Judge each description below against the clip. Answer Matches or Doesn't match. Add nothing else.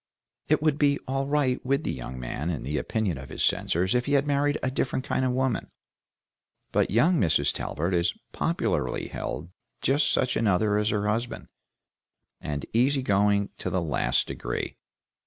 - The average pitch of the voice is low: Matches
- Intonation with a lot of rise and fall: Matches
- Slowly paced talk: Doesn't match